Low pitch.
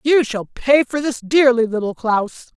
No: very high, 250 Hz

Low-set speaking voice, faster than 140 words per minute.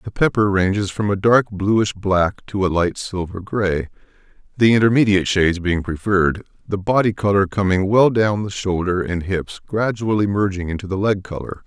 Yes: low, 100 Hz; average, 175 wpm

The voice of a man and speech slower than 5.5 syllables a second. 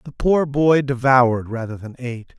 Yes: male; 4.9 syllables/s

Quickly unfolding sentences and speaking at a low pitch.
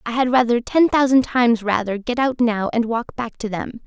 No: fast, 235 wpm; high, 235 Hz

